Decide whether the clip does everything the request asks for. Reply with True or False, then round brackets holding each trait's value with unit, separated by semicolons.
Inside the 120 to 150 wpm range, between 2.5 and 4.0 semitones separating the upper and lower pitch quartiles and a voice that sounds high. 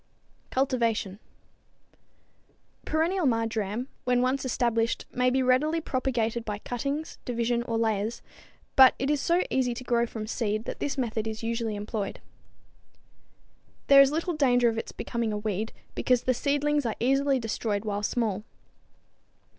True (145 wpm; 3.2 semitones; 240 Hz)